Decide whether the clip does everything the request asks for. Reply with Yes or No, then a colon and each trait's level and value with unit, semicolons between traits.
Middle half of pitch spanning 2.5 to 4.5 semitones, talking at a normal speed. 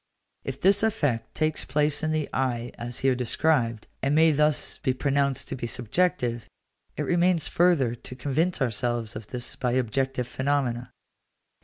Yes: average, 4.2 semitones; average, 155 wpm